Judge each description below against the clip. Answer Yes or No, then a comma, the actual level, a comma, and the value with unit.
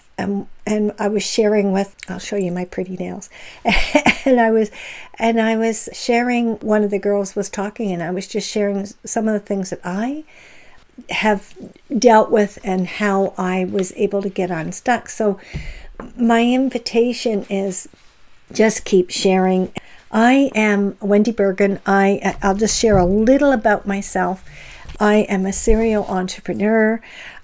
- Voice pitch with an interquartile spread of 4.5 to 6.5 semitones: No, average, 2.7 semitones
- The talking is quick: No, average, 155 wpm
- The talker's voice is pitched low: No, high, 205 Hz